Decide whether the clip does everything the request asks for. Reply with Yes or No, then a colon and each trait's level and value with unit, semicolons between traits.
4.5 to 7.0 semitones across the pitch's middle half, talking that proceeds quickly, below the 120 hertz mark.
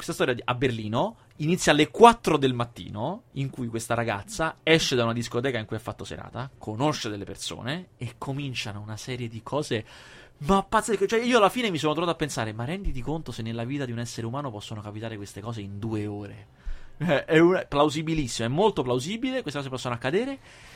No: wide, 5.6 semitones; fast, 210 wpm; low, 125 Hz